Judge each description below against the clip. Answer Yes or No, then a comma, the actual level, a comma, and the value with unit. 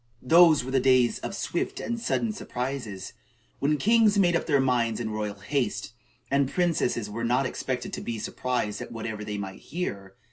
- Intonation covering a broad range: Yes, wide, 5.8 semitones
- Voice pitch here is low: Yes, low, 125 Hz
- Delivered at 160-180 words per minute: Yes, average, 175 wpm